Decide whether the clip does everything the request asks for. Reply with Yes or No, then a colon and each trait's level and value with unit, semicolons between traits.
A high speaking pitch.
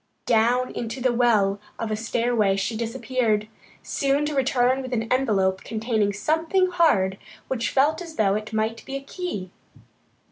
Yes: high, 235 Hz